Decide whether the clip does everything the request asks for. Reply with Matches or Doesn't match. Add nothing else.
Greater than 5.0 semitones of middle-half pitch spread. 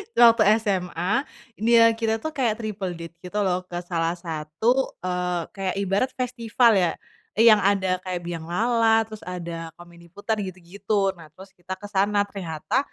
Doesn't match